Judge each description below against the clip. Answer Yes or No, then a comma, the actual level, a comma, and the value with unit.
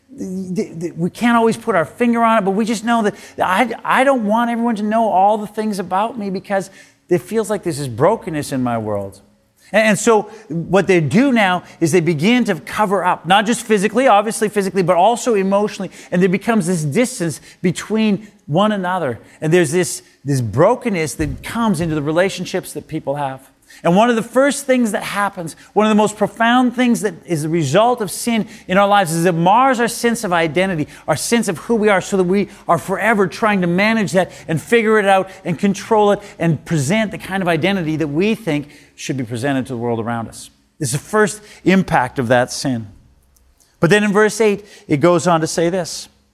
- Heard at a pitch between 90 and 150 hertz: No, high, 190 Hz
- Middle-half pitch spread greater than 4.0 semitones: Yes, average, 4.8 semitones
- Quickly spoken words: Yes, fast, 210 wpm